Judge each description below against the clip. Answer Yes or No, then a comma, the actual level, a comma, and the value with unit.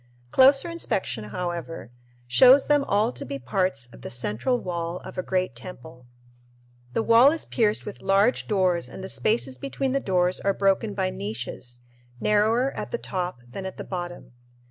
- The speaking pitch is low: No, medium, 185 Hz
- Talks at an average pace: Yes, average, 170 wpm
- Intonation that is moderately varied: No, wide, 8.1 semitones